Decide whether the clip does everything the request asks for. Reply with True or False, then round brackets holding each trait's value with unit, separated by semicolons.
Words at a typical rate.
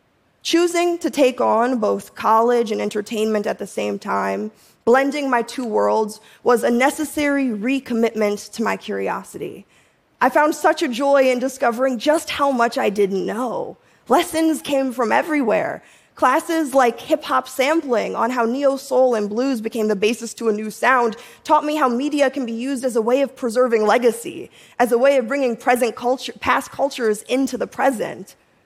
True (175 wpm)